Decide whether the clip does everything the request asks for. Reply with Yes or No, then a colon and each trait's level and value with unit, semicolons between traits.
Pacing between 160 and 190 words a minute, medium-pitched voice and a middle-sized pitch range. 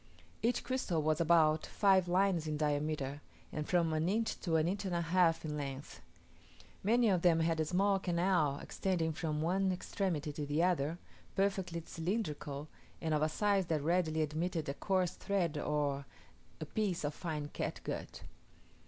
Yes: average, 165 wpm; medium, 165 Hz; average, 3.5 semitones